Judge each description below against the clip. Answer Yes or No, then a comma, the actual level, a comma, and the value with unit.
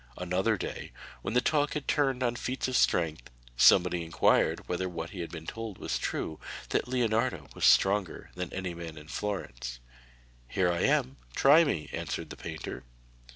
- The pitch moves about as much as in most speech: No, wide, 6.4 semitones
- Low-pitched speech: Yes, very low, 95 Hz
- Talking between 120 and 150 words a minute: No, average, 170 wpm